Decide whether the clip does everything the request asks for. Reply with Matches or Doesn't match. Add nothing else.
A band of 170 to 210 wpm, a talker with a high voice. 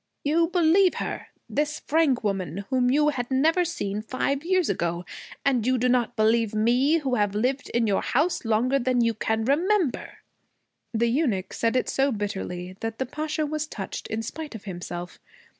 Matches